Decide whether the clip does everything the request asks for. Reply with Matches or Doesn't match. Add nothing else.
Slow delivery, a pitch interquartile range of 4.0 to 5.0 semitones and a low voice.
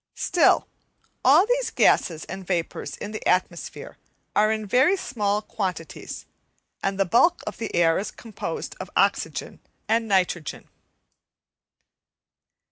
Doesn't match